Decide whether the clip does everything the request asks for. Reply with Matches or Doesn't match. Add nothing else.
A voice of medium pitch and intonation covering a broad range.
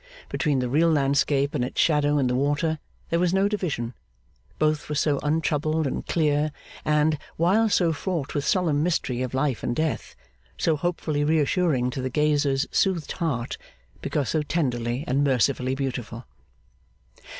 Doesn't match